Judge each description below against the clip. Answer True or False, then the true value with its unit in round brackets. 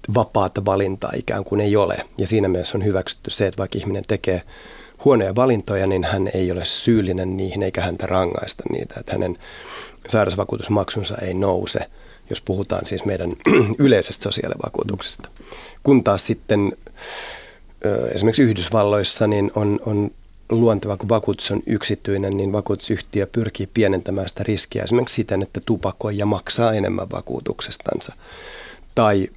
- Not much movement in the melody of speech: True (2.1 semitones)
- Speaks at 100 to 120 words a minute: False (135 wpm)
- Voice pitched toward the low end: True (100 Hz)